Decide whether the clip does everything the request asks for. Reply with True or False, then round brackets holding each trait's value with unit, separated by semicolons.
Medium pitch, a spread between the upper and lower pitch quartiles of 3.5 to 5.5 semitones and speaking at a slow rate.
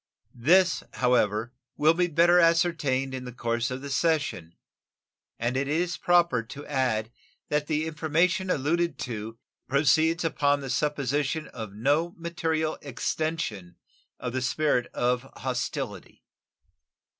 True (145 Hz; 4.8 semitones; 125 wpm)